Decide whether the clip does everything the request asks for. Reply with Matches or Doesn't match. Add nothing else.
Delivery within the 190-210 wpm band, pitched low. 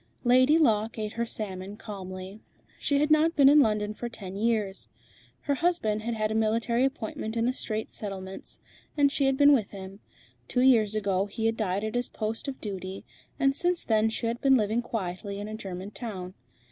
Doesn't match